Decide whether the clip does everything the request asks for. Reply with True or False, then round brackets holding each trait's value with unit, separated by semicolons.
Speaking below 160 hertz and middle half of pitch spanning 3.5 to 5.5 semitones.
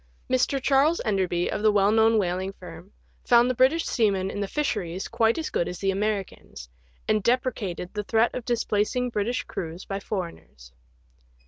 False (210 Hz; 4.2 semitones)